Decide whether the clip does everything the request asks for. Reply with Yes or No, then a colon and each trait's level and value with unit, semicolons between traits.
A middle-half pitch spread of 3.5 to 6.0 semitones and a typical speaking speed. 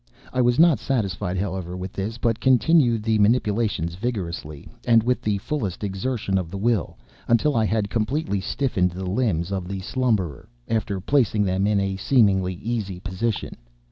Yes: average, 3.9 semitones; average, 165 wpm